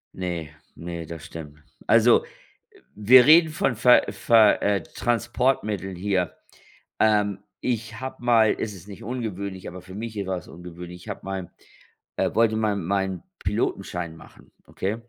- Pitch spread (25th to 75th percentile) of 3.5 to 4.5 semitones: Yes, average, 4.2 semitones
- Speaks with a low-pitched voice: Yes, low, 100 Hz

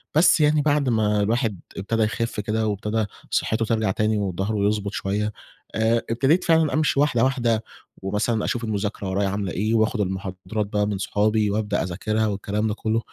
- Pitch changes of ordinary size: No, narrow, 2.0 semitones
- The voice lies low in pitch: Yes, low, 110 Hz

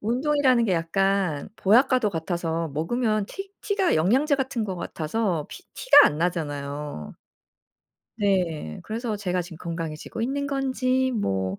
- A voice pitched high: Yes, high, 195 Hz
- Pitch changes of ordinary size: No, wide, 7.7 semitones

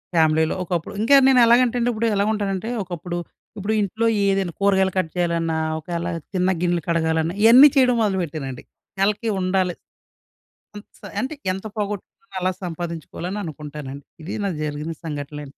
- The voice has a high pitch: No, medium, 180 Hz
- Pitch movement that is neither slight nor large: Yes, average, 4.0 semitones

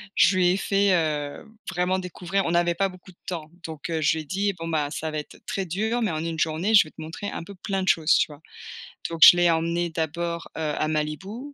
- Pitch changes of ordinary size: Yes, average, 3.1 semitones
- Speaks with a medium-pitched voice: Yes, medium, 170 Hz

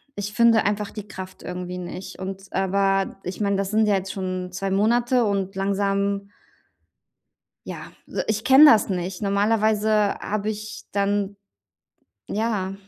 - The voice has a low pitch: No, high, 200 Hz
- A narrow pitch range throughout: Yes, narrow, 1.8 semitones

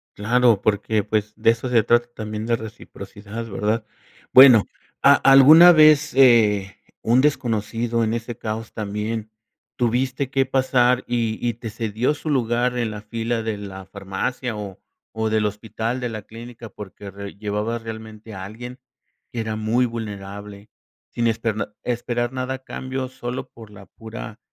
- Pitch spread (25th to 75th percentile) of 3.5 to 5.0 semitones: No, narrow, 2.5 semitones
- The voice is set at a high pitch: No, low, 115 Hz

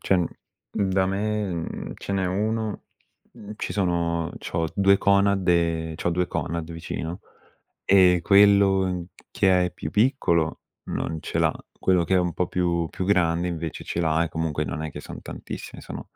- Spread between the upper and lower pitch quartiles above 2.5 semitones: Yes, average, 2.9 semitones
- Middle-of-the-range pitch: No, very low, 90 Hz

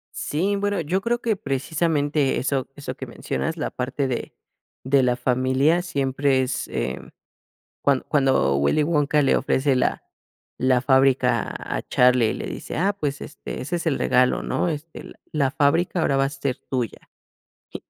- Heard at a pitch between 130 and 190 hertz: Yes, medium, 140 Hz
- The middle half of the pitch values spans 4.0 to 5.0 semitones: No, average, 3.2 semitones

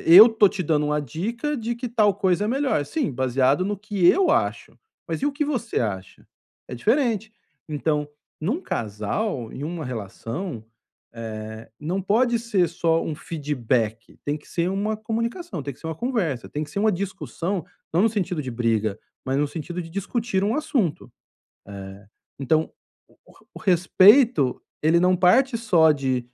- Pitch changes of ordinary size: No, wide, 7.6 semitones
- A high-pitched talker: No, medium, 175 Hz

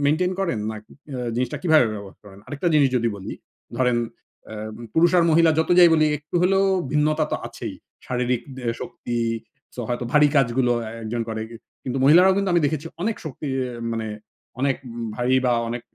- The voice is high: No, low, 135 Hz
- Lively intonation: No, average, 5.0 semitones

